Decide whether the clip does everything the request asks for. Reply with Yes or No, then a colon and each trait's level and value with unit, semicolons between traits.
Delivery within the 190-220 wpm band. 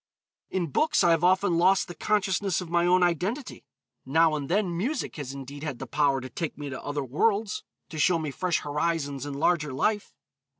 Yes: average, 200 wpm